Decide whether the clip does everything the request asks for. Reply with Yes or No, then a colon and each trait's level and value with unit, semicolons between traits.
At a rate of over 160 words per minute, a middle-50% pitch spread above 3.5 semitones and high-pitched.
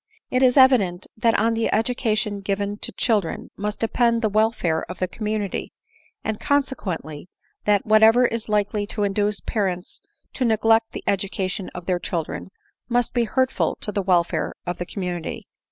No: average, 170 wpm; average, 3.2 semitones; high, 210 Hz